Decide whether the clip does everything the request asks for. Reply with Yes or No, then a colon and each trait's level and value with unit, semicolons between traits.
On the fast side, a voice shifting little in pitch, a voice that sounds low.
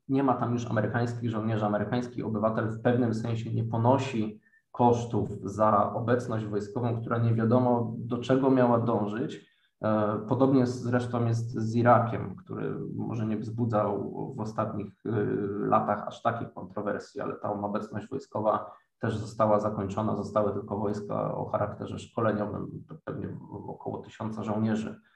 No: average, 135 wpm; narrow, 2.3 semitones; low, 110 Hz